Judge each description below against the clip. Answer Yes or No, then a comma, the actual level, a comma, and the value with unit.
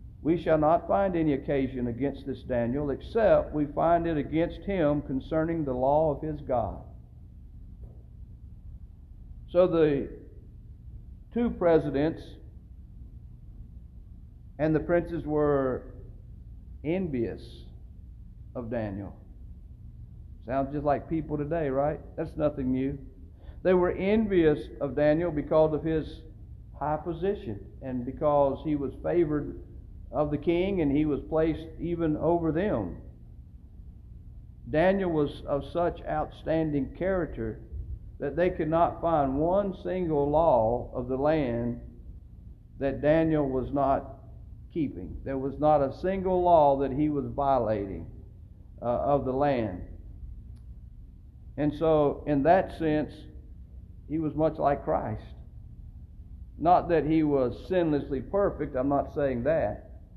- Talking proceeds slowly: Yes, slow, 120 wpm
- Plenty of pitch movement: No, average, 4.9 semitones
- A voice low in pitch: No, medium, 145 Hz